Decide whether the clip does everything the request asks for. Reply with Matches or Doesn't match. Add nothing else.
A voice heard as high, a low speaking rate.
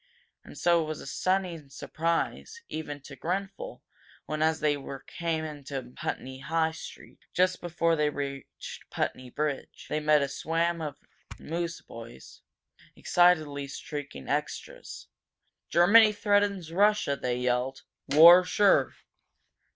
Doesn't match